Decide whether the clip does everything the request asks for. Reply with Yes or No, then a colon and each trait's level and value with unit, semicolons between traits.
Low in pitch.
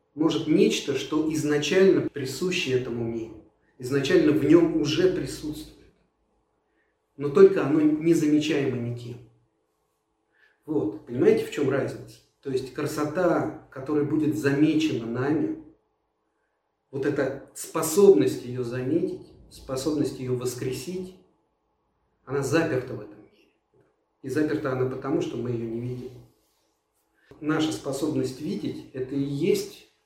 No: medium, 145 Hz